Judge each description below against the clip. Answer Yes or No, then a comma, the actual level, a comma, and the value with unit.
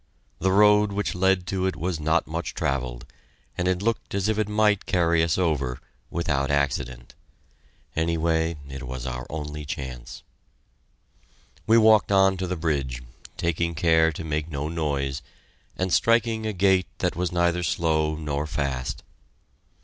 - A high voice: No, very low, 80 Hz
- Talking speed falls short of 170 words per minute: Yes, average, 150 wpm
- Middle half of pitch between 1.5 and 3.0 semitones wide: No, average, 4.6 semitones